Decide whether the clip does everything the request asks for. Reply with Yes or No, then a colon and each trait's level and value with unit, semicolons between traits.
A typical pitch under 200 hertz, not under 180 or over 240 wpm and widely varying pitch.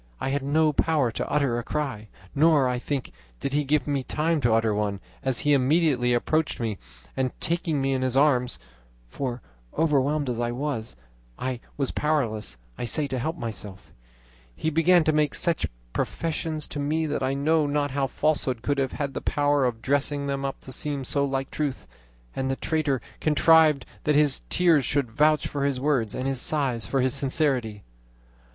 No: medium, 140 Hz; average, 185 wpm; average, 3.1 semitones